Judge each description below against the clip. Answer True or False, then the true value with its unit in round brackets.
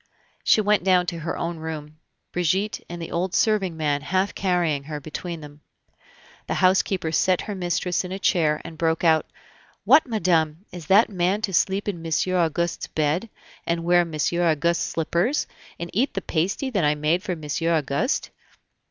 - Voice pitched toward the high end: False (170 Hz)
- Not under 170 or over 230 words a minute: True (175 wpm)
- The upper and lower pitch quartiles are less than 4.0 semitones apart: True (2.9 semitones)